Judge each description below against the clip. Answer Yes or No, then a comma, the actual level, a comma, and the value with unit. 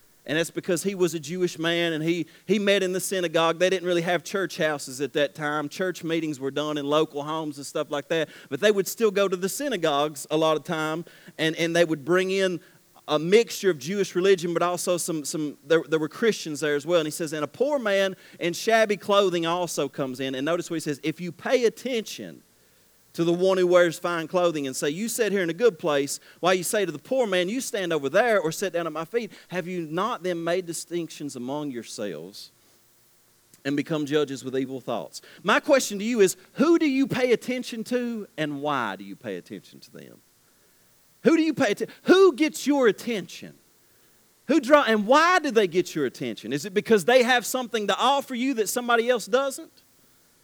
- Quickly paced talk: Yes, fast, 225 wpm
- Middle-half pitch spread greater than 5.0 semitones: Yes, wide, 5.4 semitones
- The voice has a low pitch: No, medium, 175 Hz